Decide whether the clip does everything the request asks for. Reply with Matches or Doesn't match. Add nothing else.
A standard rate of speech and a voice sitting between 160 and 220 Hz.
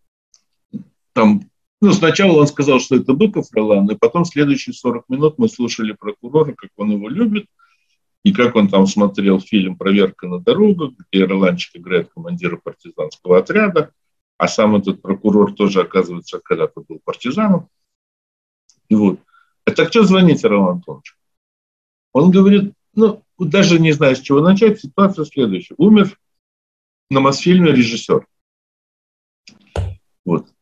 Doesn't match